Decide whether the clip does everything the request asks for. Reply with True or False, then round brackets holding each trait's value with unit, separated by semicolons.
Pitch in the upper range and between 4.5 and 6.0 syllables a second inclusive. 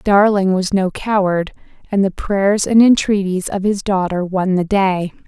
False (195 Hz; 4.2 syllables/s)